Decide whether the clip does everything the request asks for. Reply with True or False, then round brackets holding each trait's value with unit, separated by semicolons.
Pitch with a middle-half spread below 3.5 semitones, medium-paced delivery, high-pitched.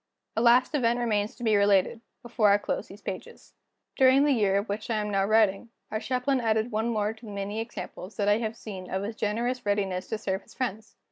False (2.7 semitones; 225 wpm; 215 Hz)